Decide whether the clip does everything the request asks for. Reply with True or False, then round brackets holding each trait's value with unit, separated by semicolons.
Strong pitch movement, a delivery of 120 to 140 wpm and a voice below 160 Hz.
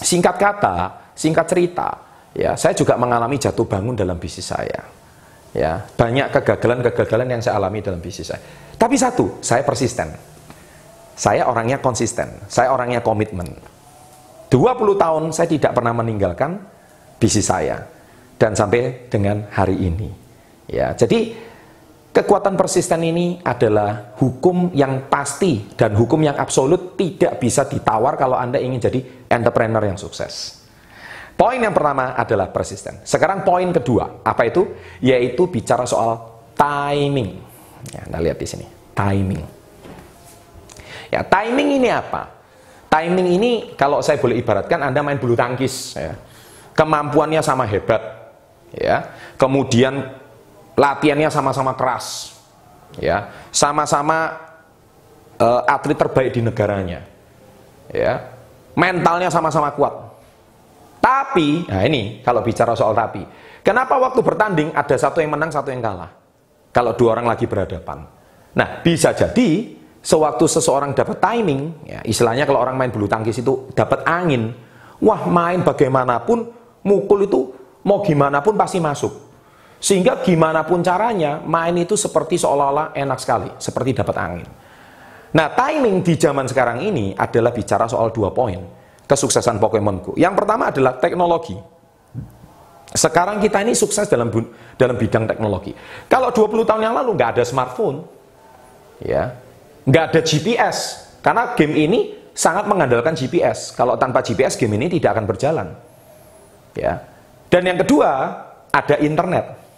True (6.5 semitones; 130 wpm; 140 Hz)